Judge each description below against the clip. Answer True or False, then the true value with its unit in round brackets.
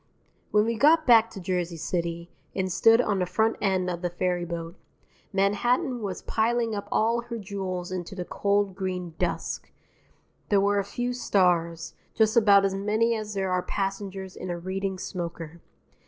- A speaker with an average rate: True (170 wpm)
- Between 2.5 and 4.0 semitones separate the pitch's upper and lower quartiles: True (3.3 semitones)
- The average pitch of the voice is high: True (195 Hz)